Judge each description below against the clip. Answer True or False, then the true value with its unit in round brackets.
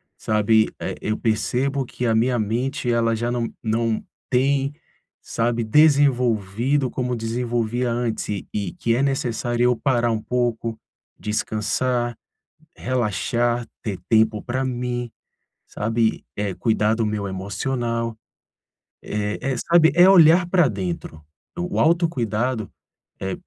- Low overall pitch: True (120 Hz)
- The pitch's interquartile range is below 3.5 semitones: True (2.8 semitones)